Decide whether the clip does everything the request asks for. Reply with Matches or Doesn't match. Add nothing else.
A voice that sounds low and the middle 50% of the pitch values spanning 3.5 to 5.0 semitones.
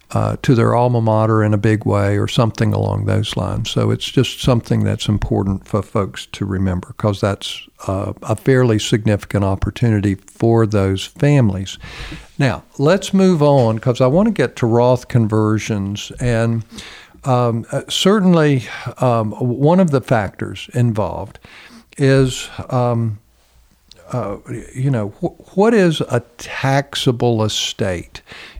Matches